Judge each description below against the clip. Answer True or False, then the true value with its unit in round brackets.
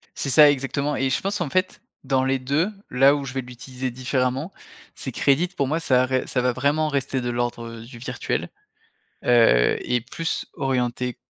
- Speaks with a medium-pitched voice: False (130 Hz)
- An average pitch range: False (2.2 semitones)